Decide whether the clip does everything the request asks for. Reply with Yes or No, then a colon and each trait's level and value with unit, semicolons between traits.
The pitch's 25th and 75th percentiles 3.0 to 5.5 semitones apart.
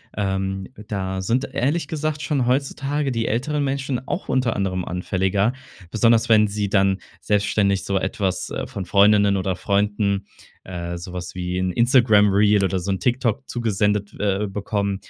Yes: average, 3.6 semitones